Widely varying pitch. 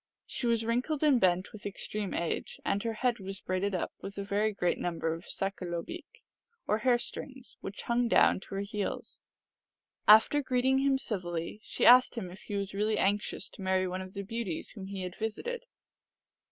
No: average, 4.1 semitones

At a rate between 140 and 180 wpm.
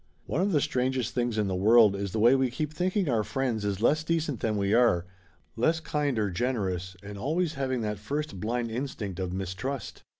No: fast, 205 wpm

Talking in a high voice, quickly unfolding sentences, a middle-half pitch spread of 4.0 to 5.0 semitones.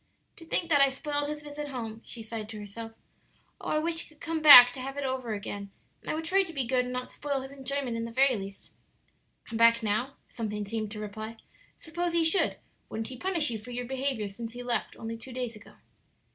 Yes: very high, 250 Hz; fast, 235 wpm; average, 4.3 semitones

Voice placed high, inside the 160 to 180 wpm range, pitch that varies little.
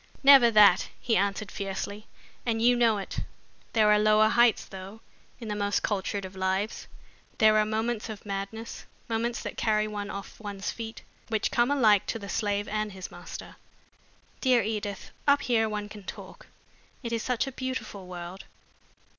Yes: high, 215 Hz; average, 170 wpm; narrow, 2.3 semitones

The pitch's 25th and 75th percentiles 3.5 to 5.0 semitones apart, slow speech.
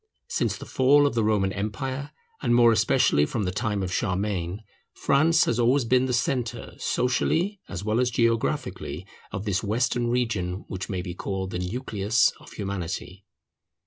No: average, 4.4 semitones; average, 165 wpm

